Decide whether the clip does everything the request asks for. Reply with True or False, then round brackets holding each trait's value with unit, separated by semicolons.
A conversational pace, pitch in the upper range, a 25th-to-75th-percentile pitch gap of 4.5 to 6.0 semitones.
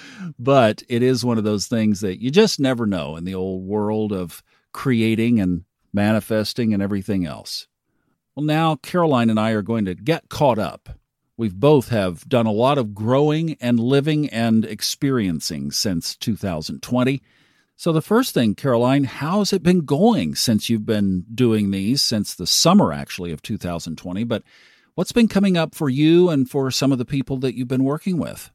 False (180 wpm; 120 Hz; 5.3 semitones)